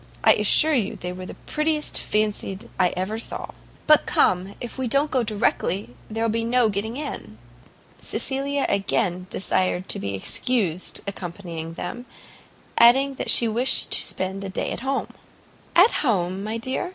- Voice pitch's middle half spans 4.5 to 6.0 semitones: Yes, wide, 5.6 semitones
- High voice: Yes, high, 215 Hz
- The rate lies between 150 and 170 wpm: Yes, average, 165 wpm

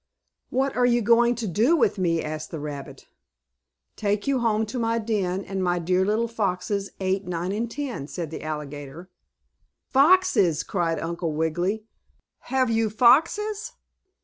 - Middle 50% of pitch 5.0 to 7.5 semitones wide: Yes, wide, 5.5 semitones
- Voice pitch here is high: Yes, high, 205 Hz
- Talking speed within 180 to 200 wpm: No, average, 150 wpm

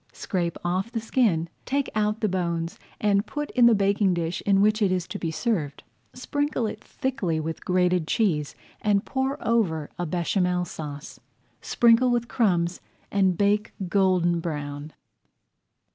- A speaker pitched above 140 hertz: Yes, high, 190 Hz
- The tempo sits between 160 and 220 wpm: No, average, 150 wpm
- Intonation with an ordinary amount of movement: Yes, average, 4.6 semitones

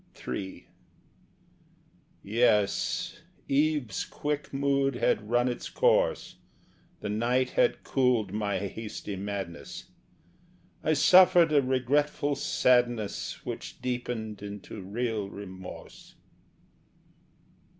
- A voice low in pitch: Yes, low, 120 Hz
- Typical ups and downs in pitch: Yes, average, 4.9 semitones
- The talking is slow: Yes, slow, 90 wpm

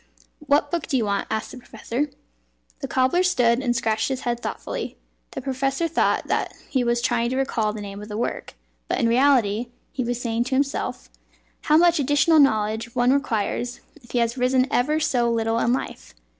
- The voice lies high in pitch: Yes, high, 245 Hz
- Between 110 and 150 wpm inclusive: No, average, 195 wpm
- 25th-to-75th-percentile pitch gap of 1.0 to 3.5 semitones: Yes, average, 2.9 semitones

